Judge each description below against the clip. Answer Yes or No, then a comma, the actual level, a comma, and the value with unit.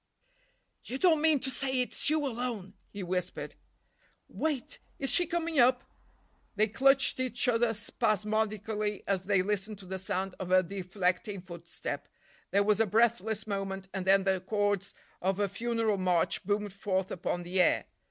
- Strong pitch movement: No, average, 3.9 semitones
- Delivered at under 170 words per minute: Yes, average, 150 wpm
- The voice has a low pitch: No, high, 205 Hz